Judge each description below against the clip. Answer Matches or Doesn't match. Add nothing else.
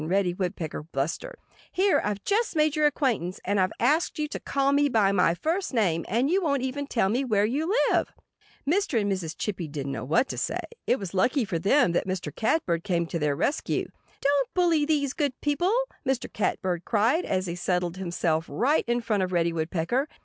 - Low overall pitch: Doesn't match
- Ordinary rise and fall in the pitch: Doesn't match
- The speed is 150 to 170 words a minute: Doesn't match